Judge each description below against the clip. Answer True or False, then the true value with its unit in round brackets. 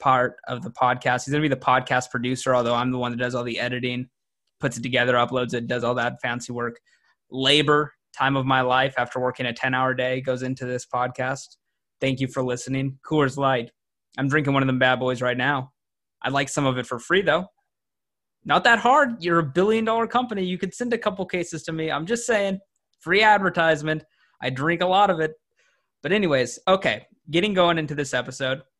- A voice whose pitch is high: False (130 Hz)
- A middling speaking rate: False (215 wpm)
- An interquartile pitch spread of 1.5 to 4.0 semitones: False (4.7 semitones)